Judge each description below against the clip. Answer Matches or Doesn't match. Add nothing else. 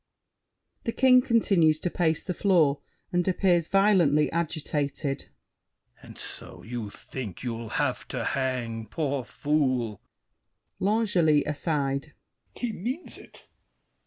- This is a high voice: Doesn't match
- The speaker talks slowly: Matches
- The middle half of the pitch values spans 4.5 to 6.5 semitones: Matches